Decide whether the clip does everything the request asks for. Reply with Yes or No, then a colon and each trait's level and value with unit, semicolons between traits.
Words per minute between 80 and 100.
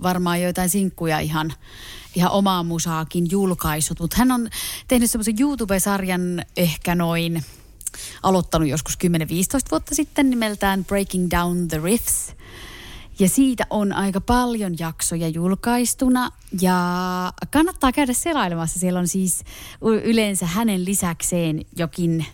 No: average, 120 wpm